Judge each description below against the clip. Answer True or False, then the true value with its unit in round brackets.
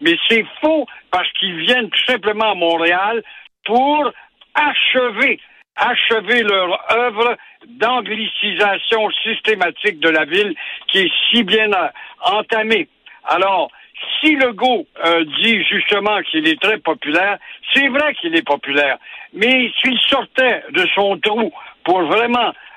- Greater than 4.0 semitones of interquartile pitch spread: True (4.4 semitones)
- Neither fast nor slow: False (125 wpm)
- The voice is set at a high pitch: True (220 Hz)